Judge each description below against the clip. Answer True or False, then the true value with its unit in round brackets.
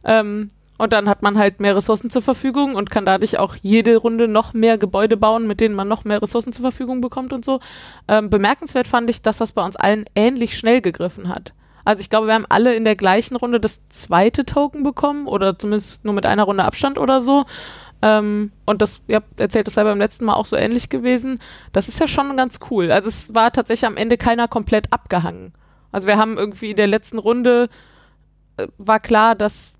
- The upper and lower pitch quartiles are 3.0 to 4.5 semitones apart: False (2.6 semitones)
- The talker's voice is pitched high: True (220 Hz)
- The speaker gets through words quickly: True (220 wpm)